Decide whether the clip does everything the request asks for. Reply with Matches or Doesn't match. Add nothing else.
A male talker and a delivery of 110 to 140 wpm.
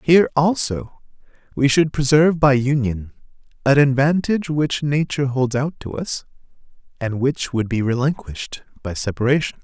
Matches